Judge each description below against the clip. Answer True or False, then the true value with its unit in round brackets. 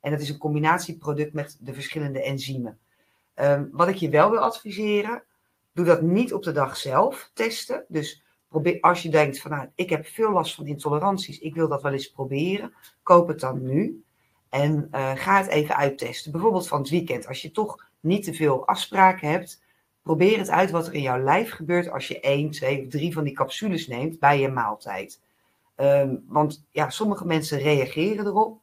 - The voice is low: False (155 Hz)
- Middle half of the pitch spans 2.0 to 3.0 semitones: False (3.9 semitones)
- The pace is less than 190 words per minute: False (195 wpm)